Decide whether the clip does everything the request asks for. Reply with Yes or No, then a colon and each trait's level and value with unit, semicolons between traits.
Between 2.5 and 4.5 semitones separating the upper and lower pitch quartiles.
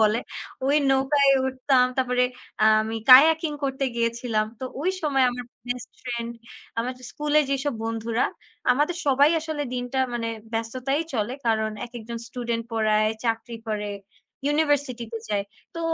Yes: average, 3.4 semitones